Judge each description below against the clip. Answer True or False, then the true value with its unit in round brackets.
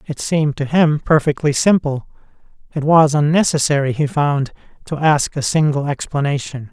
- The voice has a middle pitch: True (145 Hz)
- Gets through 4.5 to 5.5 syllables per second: True (5.0 syllables/s)